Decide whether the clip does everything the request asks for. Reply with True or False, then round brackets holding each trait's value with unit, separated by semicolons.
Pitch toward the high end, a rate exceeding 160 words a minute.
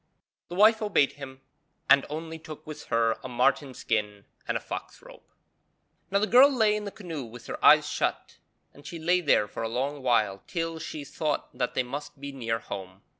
False (140 Hz; 200 wpm)